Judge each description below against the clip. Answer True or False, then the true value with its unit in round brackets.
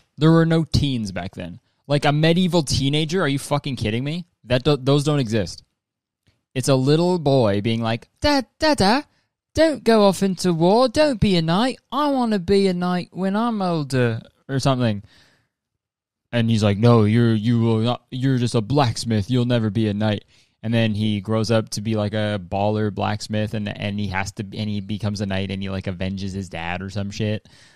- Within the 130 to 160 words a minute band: False (205 wpm)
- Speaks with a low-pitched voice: True (120 Hz)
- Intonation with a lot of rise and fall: True (7.4 semitones)